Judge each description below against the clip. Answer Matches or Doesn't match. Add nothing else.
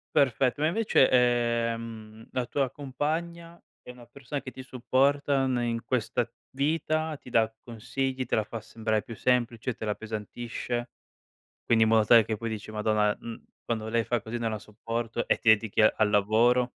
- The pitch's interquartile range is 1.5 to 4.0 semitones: Matches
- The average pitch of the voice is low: Matches